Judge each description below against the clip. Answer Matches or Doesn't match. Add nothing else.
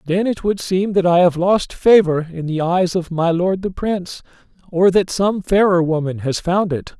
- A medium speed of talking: Doesn't match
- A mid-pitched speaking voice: Matches